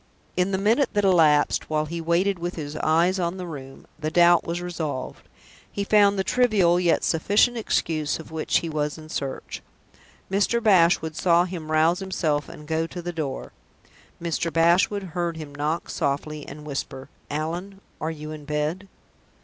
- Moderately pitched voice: Yes, medium, 165 Hz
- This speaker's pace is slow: No, average, 170 wpm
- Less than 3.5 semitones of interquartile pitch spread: Yes, average, 3.1 semitones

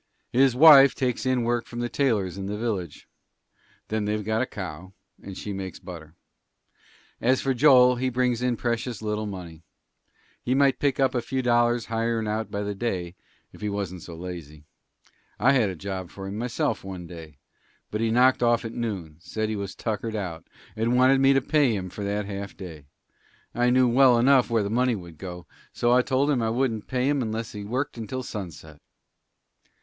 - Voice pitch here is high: No, low, 110 Hz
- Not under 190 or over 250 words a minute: Yes, average, 200 wpm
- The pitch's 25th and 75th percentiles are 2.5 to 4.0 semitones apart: No, average, 4.4 semitones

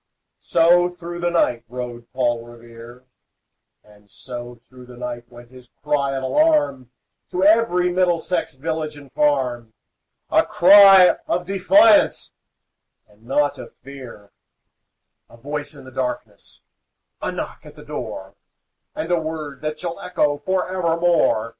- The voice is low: No, medium, 145 Hz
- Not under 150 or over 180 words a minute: No, slow, 135 wpm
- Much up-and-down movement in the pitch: Yes, wide, 6.2 semitones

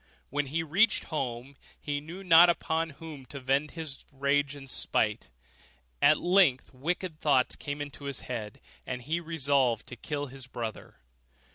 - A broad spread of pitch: No, average, 3.5 semitones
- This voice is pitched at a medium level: Yes, medium, 145 Hz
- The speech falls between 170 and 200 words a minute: No, average, 160 wpm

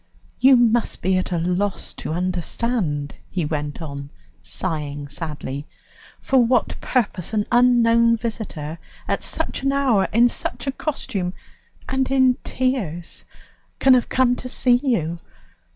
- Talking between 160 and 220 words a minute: No, slow, 135 wpm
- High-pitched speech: Yes, high, 215 Hz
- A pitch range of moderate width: No, wide, 7.1 semitones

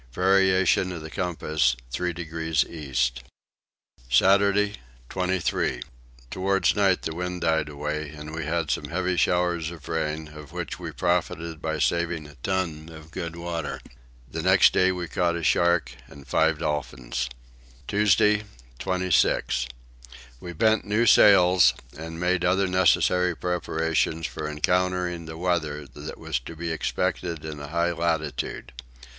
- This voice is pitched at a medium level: No, very low, 85 Hz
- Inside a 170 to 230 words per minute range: No, average, 140 wpm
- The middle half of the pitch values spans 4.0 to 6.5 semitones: No, average, 2.8 semitones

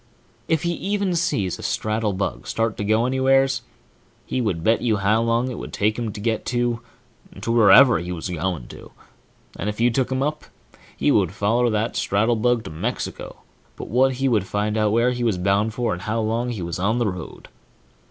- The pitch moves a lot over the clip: No, average, 3.3 semitones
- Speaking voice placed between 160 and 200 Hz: No, low, 115 Hz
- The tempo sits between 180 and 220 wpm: Yes, average, 195 wpm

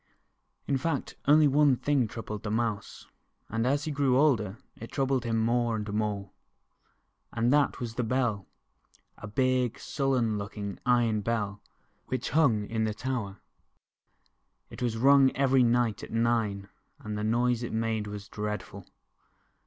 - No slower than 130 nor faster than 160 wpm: Yes, average, 155 wpm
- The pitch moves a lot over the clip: No, average, 3.5 semitones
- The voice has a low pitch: Yes, low, 115 Hz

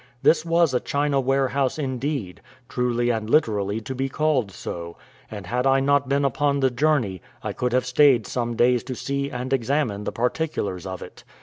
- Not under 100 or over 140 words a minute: No, average, 185 wpm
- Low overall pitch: Yes, low, 130 Hz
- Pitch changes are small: No, average, 3.4 semitones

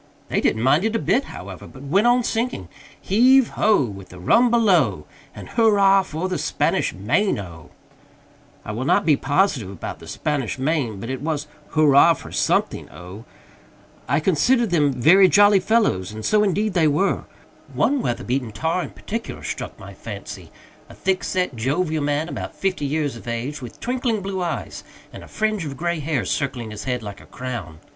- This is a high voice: No, medium, 155 Hz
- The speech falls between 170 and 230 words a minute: Yes, average, 185 wpm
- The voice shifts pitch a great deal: Yes, wide, 8.2 semitones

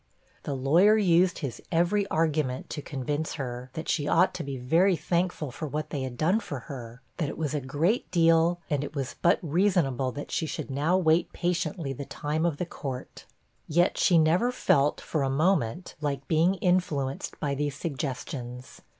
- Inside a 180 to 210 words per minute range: Yes, average, 185 wpm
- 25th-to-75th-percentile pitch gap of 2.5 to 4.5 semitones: Yes, average, 4.0 semitones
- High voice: No, medium, 155 Hz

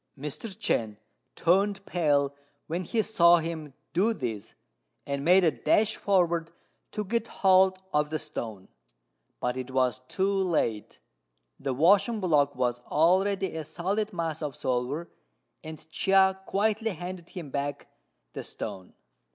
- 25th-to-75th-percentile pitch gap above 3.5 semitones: Yes, average, 5.2 semitones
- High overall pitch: No, medium, 165 Hz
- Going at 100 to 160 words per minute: Yes, slow, 135 wpm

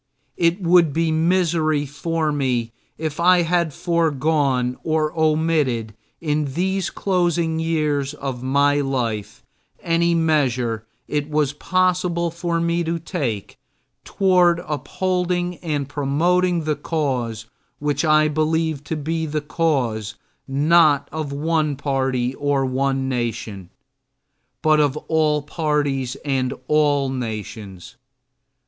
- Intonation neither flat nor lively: Yes, average, 3.6 semitones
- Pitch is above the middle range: No, medium, 150 Hz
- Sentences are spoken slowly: Yes, slow, 115 wpm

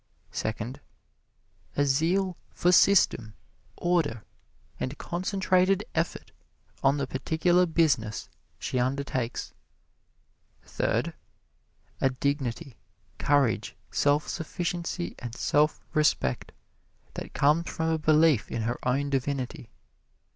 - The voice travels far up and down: No, average, 4.8 semitones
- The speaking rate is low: Yes, slow, 95 wpm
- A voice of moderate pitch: Yes, medium, 145 Hz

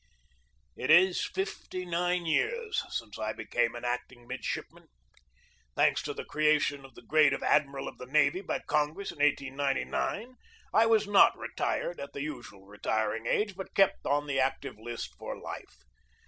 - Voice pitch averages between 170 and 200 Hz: No, medium, 145 Hz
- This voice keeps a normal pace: Yes, average, 160 wpm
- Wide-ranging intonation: Yes, wide, 6.1 semitones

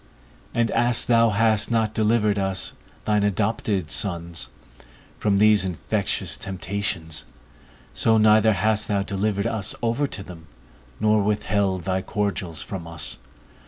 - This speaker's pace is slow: Yes, slow, 125 wpm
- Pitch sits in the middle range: No, low, 105 Hz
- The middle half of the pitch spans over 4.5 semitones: No, narrow, 2.4 semitones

